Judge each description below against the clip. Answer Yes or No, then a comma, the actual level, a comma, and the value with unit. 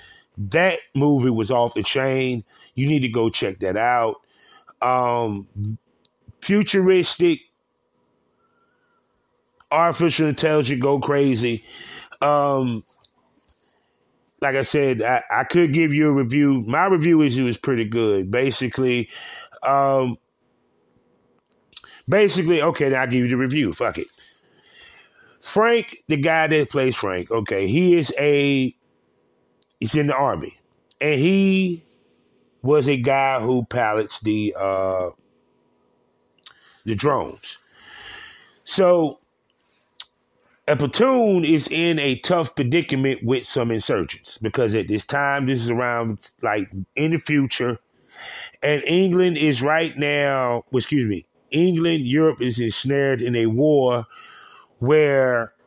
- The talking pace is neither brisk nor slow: No, slow, 120 wpm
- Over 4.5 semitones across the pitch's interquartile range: Yes, wide, 5.6 semitones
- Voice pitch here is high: No, medium, 140 Hz